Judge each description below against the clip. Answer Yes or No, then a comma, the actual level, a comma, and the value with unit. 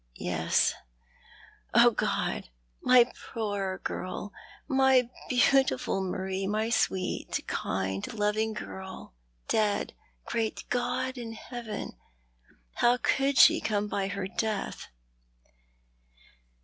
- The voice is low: No, high, 215 Hz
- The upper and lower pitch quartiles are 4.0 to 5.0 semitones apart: Yes, average, 4.3 semitones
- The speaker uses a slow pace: Yes, slow, 100 wpm